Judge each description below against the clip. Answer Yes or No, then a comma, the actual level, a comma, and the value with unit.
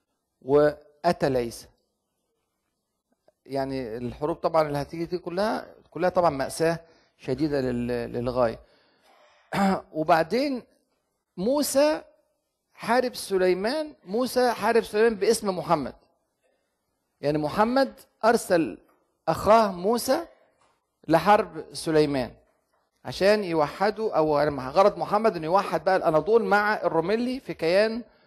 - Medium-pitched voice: Yes, medium, 180 Hz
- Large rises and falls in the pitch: Yes, wide, 6.4 semitones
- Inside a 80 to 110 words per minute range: Yes, average, 90 wpm